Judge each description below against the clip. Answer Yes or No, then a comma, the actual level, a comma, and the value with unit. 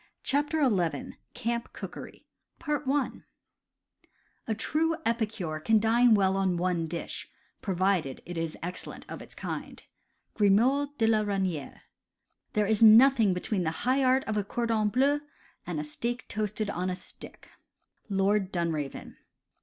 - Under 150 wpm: Yes, average, 140 wpm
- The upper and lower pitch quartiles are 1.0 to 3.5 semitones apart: No, average, 4.5 semitones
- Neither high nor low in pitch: No, high, 210 Hz